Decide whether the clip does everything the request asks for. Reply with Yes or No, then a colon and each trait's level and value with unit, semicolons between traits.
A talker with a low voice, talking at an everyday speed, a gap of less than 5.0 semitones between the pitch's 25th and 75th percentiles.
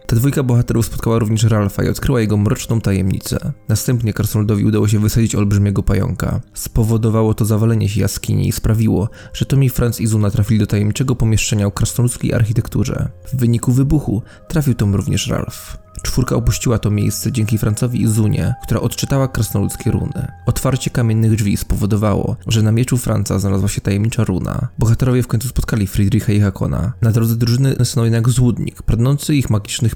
Yes: low, 115 Hz; average, 170 wpm; average, 2.7 semitones